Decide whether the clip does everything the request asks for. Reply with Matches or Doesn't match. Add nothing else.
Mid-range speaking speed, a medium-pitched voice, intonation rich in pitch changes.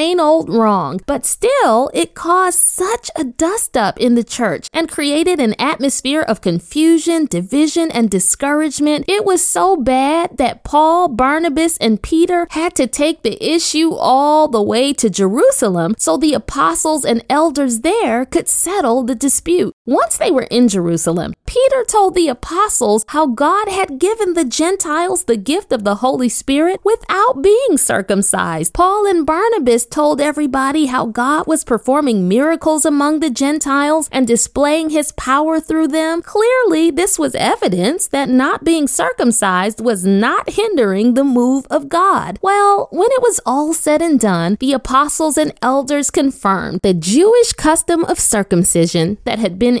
Doesn't match